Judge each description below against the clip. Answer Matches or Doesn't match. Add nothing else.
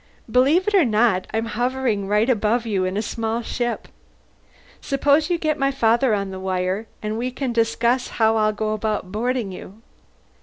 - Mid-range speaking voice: Doesn't match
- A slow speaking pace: Doesn't match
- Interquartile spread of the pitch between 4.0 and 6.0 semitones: Doesn't match